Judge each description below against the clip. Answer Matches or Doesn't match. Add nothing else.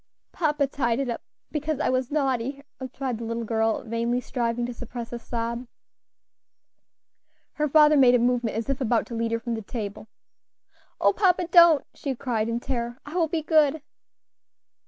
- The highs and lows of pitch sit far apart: Doesn't match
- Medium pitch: Doesn't match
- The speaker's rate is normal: Matches